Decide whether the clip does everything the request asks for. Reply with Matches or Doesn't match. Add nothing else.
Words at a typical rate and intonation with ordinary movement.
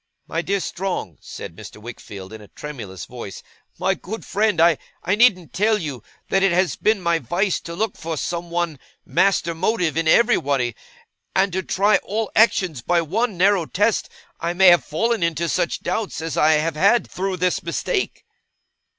Matches